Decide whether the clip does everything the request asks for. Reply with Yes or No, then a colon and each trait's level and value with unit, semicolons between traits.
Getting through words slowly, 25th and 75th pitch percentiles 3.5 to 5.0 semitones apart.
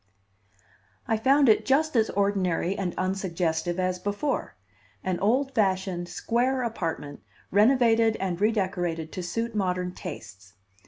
Yes: slow, 120 wpm; average, 4.3 semitones